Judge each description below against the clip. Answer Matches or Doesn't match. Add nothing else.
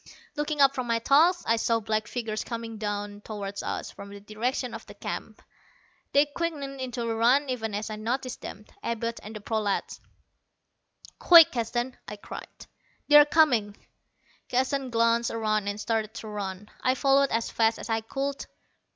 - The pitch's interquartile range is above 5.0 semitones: Doesn't match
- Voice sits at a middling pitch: Doesn't match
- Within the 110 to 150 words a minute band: Doesn't match